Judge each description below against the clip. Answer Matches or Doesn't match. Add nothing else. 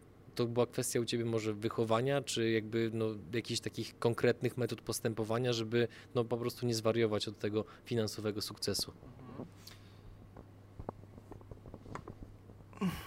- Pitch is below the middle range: Matches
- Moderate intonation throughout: Doesn't match